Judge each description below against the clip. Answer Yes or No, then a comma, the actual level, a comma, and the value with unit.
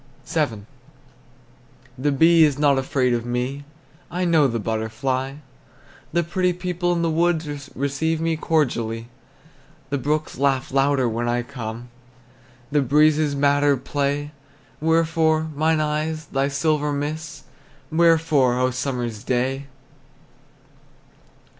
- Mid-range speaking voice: Yes, medium, 145 Hz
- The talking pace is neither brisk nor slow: No, slow, 115 wpm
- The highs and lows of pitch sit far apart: No, average, 3.5 semitones